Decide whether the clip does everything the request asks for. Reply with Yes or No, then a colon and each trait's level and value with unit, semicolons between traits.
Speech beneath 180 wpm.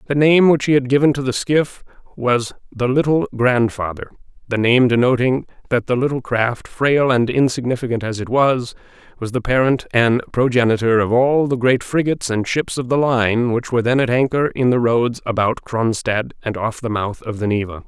No: average, 195 wpm